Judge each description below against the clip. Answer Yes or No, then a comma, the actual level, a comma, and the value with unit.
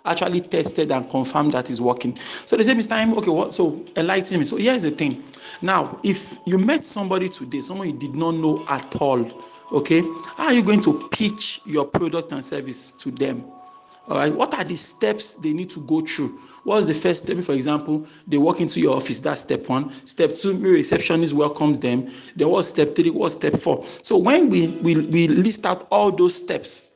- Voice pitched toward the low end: No, medium, 170 Hz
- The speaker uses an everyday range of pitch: No, wide, 6.0 semitones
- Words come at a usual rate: No, fast, 210 wpm